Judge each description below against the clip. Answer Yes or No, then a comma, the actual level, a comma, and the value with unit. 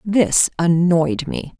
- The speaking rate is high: No, slow, 115 wpm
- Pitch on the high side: No, medium, 175 Hz